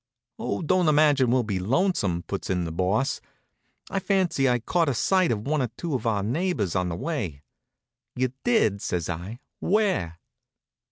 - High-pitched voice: No, low, 125 Hz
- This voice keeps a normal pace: Yes, average, 170 wpm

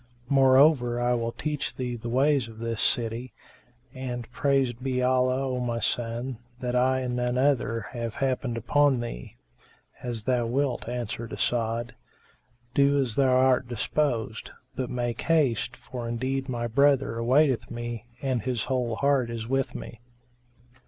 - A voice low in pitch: Yes, low, 125 Hz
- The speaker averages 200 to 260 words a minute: No, average, 150 wpm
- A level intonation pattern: Yes, narrow, 2.1 semitones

